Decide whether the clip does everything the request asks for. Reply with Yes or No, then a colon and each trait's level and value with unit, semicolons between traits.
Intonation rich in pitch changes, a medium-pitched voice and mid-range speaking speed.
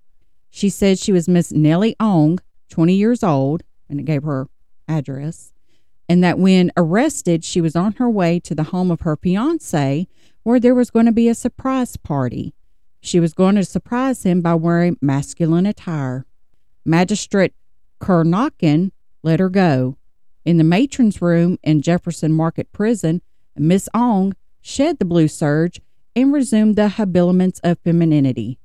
No: average, 4.5 semitones; medium, 175 Hz; average, 155 wpm